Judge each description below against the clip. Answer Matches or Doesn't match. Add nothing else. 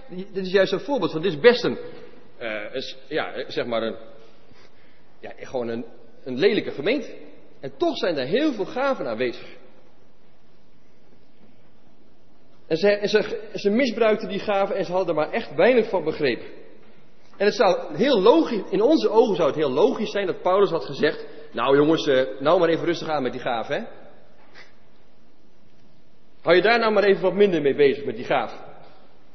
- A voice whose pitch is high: Matches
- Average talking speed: Matches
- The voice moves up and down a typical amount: Doesn't match